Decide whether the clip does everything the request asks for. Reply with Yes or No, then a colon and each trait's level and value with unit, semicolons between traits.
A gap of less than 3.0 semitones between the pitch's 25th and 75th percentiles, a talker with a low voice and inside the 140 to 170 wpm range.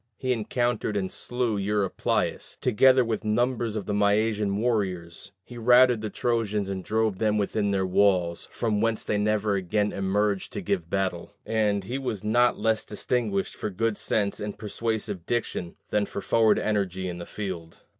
Yes: narrow, 2.4 semitones; low, 105 Hz; average, 165 wpm